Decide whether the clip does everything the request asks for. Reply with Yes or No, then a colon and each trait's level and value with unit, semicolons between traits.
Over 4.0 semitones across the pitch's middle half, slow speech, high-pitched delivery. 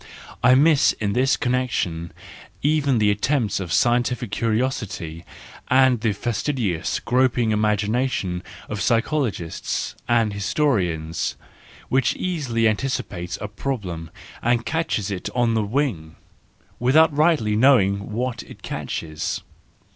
No: average, 4.5 semitones; slow, 115 wpm; low, 115 Hz